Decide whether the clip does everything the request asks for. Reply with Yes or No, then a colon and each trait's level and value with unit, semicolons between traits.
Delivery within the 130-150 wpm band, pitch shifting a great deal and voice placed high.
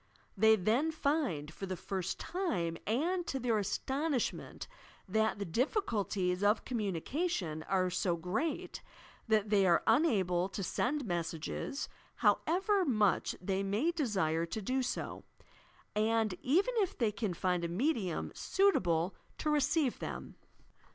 Yes: slow, 135 wpm; wide, 7.8 semitones; high, 215 Hz